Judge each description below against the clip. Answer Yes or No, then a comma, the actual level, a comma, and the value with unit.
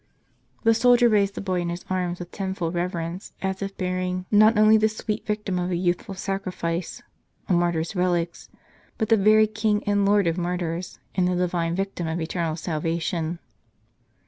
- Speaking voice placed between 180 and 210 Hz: Yes, medium, 185 Hz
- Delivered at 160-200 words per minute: Yes, average, 175 wpm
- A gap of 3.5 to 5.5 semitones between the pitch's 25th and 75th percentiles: No, average, 2.9 semitones